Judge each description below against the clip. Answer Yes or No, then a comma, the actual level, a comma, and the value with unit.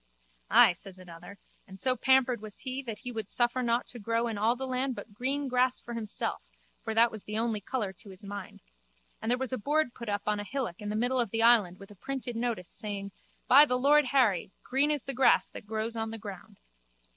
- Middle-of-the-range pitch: No, high, 230 Hz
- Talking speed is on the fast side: Yes, fast, 235 wpm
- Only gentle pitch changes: No, average, 3.7 semitones